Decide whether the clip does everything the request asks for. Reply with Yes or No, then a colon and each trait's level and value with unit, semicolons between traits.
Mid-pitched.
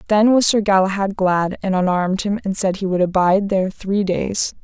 No: high, 195 Hz